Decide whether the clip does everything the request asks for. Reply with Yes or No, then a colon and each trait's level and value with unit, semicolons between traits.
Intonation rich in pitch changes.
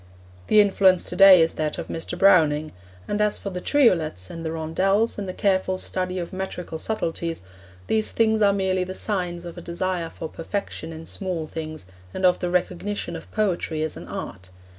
No: average, 3.2 semitones